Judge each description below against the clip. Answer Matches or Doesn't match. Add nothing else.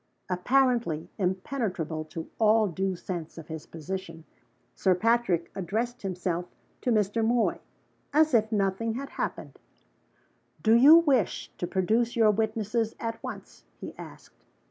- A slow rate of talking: Matches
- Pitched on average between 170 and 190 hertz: Doesn't match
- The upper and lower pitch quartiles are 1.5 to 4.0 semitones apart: Doesn't match